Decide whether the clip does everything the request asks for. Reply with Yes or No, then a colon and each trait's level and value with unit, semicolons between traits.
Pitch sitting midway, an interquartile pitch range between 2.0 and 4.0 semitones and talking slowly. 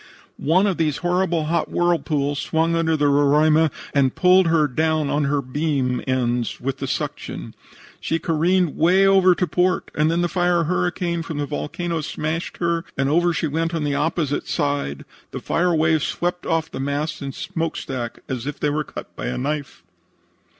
No: medium, 160 Hz; average, 3.1 semitones; average, 180 wpm